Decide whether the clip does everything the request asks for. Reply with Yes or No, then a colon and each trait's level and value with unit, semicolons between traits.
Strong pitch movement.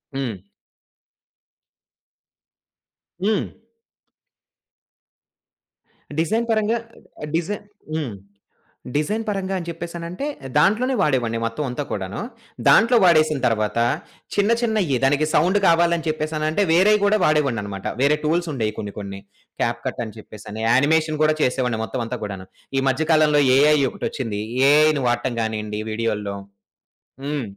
Yes: wide, 6.9 semitones